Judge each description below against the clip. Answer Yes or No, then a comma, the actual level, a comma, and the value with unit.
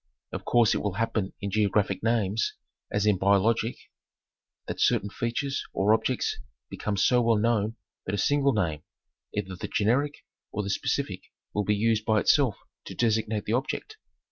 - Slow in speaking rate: No, average, 165 wpm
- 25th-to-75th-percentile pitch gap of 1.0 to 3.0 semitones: Yes, narrow, 2.5 semitones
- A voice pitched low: Yes, low, 110 Hz